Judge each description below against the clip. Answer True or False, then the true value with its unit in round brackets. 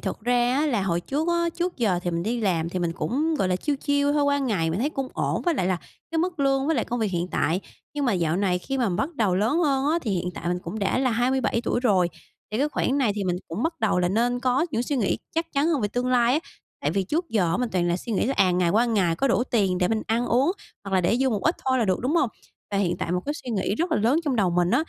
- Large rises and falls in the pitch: True (6.8 semitones)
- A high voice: True (235 Hz)